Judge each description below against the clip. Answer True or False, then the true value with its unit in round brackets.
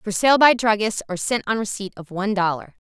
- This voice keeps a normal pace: False (230 wpm)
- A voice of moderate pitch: False (205 Hz)